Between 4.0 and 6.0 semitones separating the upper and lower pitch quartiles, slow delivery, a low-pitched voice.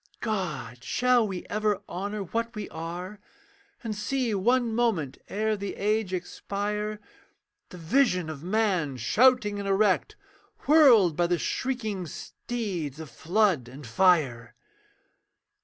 No: average, 4.4 semitones; slow, 125 wpm; high, 200 Hz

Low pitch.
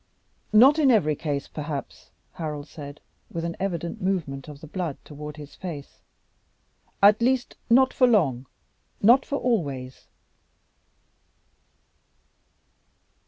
No: medium, 165 Hz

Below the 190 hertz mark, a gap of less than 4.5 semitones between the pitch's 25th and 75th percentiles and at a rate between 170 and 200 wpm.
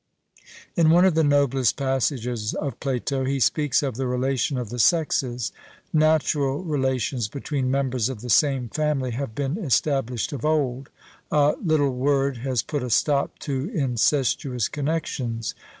No: low, 135 Hz; average, 2.9 semitones; average, 150 wpm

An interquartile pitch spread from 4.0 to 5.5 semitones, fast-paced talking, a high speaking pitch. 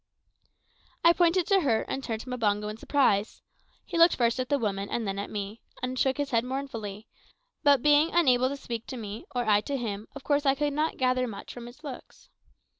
Yes: average, 4.5 semitones; fast, 215 wpm; very high, 255 Hz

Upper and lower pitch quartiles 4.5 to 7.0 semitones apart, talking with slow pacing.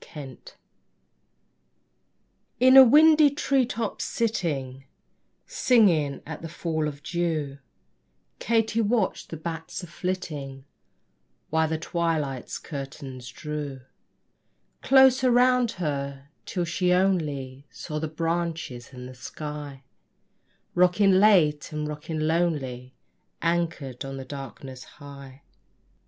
Yes: average, 4.8 semitones; slow, 110 wpm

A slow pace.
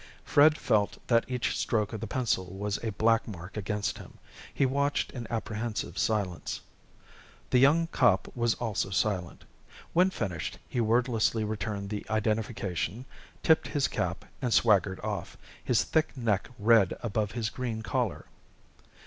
No: average, 145 wpm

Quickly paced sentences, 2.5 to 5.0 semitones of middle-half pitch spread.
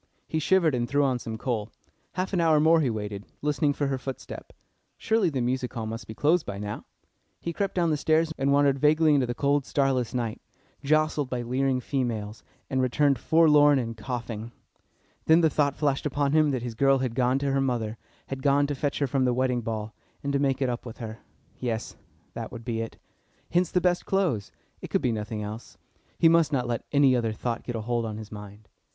Yes: fast, 220 wpm; average, 4.0 semitones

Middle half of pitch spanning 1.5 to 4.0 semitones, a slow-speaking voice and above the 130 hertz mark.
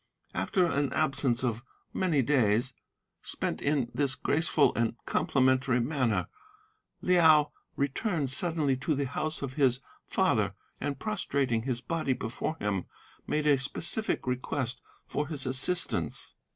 Yes: average, 3.6 semitones; slow, 125 wpm; medium, 140 Hz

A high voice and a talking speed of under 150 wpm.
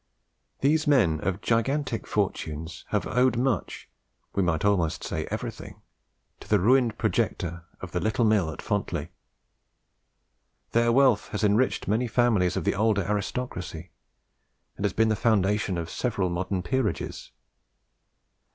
No: low, 105 Hz; slow, 135 wpm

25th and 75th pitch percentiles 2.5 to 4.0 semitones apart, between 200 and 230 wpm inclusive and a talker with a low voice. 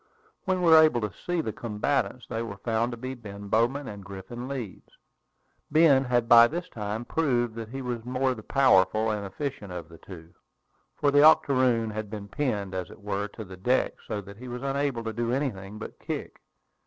No: average, 4.5 semitones; fast, 205 wpm; low, 115 Hz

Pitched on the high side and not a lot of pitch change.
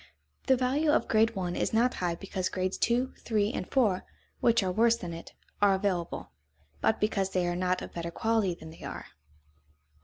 No: high, 200 Hz; average, 4.2 semitones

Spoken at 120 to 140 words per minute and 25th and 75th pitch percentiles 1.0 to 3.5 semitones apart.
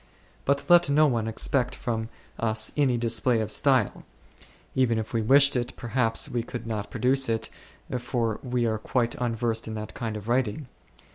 No: average, 170 wpm; narrow, 2.4 semitones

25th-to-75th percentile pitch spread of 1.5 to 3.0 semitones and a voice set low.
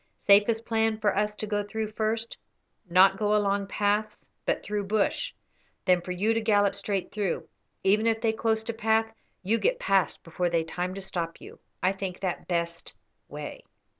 No: narrow, 2.6 semitones; high, 205 Hz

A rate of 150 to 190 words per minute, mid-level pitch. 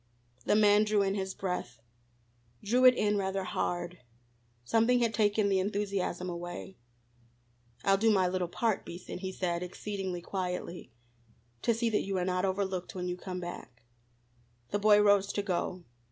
No: average, 160 wpm; high, 195 Hz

